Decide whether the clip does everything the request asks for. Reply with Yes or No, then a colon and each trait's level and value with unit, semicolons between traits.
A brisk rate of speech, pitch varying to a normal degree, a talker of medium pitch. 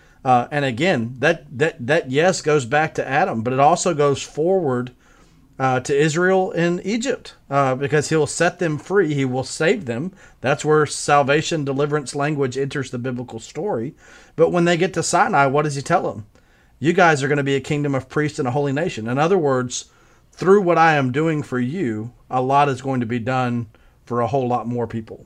Yes: fast, 210 wpm; average, 3.7 semitones; medium, 145 Hz